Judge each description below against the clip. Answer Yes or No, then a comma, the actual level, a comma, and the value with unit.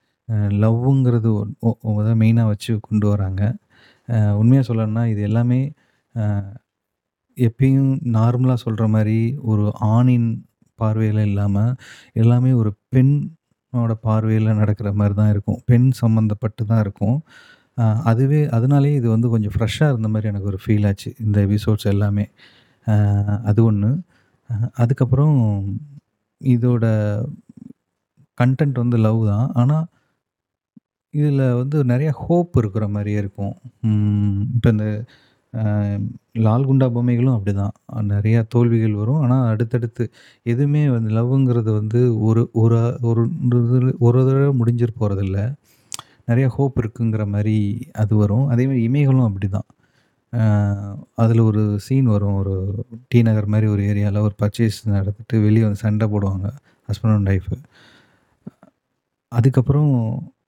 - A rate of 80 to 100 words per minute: No, average, 110 wpm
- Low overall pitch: Yes, low, 115 Hz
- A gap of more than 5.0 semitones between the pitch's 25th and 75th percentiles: No, average, 3.1 semitones